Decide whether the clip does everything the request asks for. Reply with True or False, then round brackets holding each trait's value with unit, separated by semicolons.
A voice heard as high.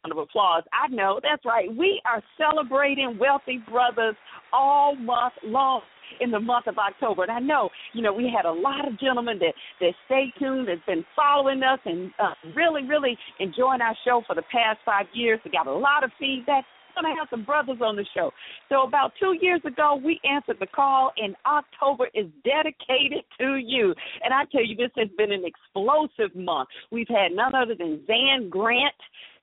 True (255 Hz)